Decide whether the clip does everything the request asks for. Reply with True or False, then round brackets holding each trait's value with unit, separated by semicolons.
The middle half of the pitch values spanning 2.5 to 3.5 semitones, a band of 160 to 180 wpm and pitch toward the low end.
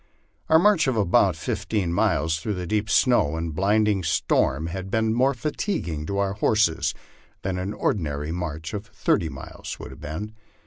False (5.0 semitones; 165 wpm; 95 Hz)